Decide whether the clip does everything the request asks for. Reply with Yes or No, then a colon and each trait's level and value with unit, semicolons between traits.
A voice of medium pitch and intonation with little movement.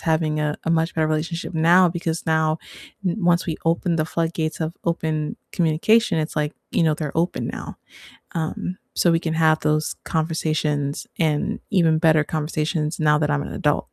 Yes: medium, 160 Hz; narrow, 1.3 semitones